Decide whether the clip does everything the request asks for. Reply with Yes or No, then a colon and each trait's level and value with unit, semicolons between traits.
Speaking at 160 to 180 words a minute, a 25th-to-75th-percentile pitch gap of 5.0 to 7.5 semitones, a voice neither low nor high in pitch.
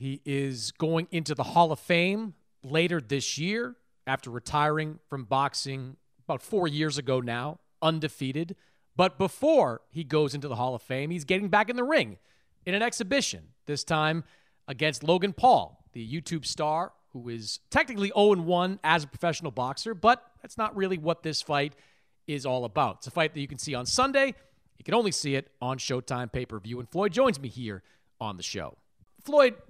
No: average, 190 wpm; wide, 5.6 semitones; medium, 155 Hz